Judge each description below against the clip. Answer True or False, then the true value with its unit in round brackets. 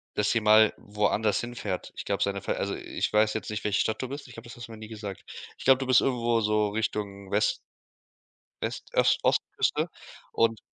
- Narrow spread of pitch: True (1.8 semitones)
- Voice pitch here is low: True (110 Hz)